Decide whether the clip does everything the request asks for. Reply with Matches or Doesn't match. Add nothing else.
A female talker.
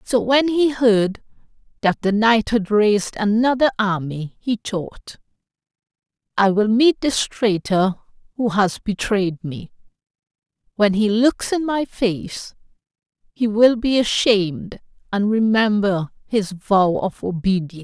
Matches